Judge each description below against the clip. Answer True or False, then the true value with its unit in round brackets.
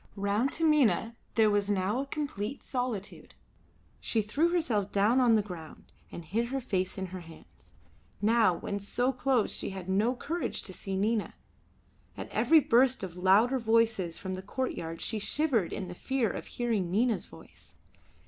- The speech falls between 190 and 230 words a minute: False (165 wpm)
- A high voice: True (215 Hz)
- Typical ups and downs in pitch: True (4.7 semitones)